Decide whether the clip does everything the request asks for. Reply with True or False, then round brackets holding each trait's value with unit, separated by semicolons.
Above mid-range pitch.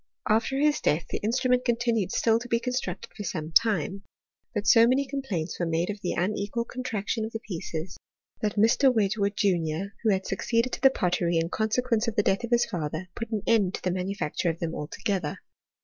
True (210 Hz)